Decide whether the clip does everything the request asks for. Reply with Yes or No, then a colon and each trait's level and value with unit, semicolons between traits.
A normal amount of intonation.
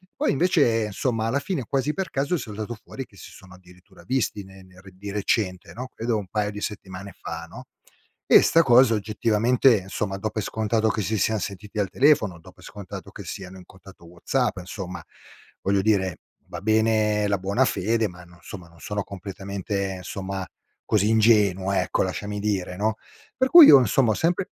Yes: average, 3.0 semitones